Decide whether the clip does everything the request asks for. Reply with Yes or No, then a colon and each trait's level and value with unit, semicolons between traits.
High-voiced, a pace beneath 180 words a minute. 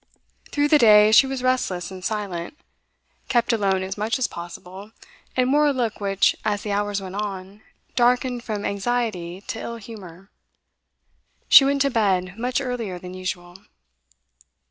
Yes: high, 210 Hz; average, 155 wpm